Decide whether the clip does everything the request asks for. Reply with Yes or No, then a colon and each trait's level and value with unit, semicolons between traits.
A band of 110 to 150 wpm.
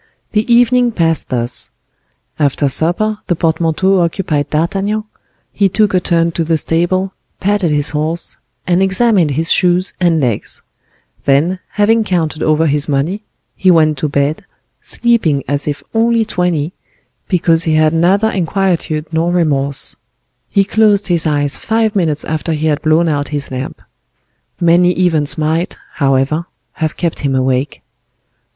Yes: average, 145 wpm